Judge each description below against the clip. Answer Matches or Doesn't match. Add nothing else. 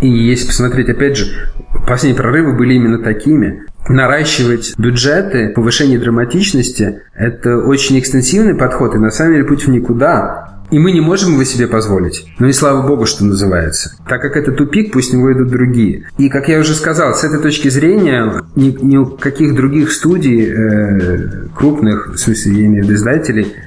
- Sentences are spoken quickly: Matches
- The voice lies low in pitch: Matches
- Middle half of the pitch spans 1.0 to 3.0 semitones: Doesn't match